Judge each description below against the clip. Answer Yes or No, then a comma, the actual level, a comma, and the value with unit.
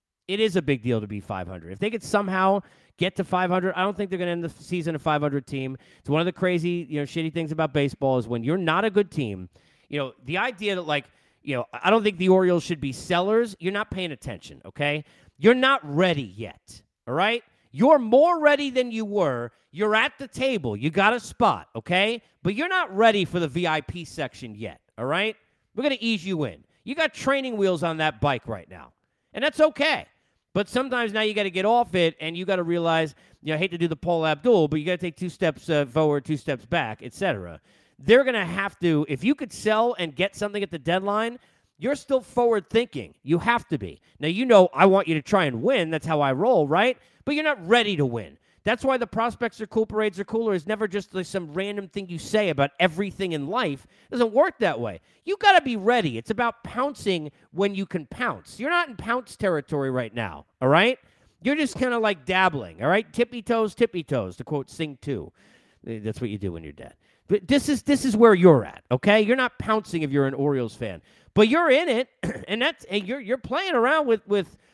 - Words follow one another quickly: Yes, fast, 240 wpm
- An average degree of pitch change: No, wide, 7.5 semitones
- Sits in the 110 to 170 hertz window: No, medium, 185 Hz